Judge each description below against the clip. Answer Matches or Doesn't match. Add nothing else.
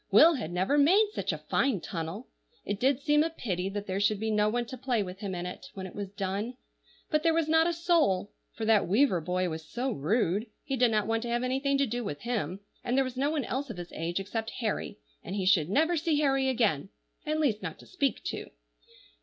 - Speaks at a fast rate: Matches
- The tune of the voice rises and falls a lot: Matches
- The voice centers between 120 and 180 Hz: Doesn't match